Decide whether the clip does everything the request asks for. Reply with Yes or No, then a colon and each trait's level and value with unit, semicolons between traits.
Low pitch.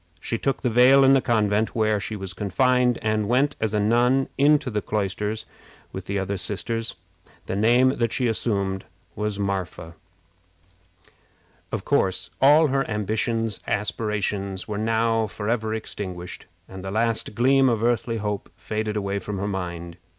Yes: low, 110 Hz